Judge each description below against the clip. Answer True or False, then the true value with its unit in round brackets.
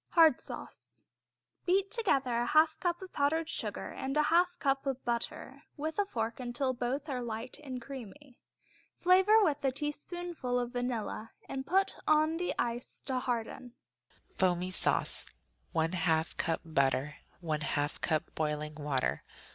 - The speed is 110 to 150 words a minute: True (145 wpm)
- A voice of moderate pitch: False (255 Hz)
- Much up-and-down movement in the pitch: True (7.0 semitones)